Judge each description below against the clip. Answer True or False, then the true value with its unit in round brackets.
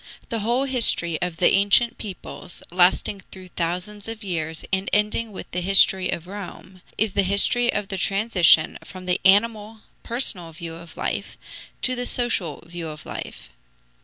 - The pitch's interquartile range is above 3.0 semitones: True (3.7 semitones)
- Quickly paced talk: False (160 wpm)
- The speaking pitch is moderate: False (195 Hz)